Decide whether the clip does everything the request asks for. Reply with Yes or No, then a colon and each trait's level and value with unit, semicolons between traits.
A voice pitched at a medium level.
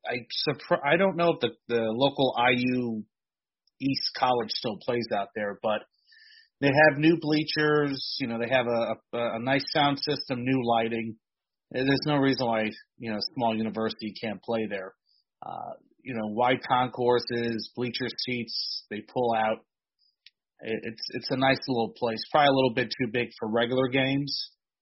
No: low, 125 Hz